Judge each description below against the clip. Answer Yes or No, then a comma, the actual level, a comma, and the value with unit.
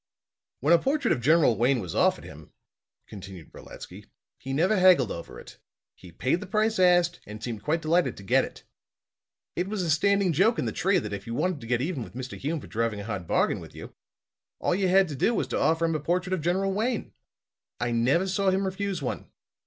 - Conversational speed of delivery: No, fast, 225 wpm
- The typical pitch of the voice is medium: Yes, medium, 165 Hz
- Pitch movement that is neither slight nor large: No, wide, 7.9 semitones